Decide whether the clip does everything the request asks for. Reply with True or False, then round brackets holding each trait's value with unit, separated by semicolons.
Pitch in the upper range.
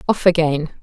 False (165 Hz)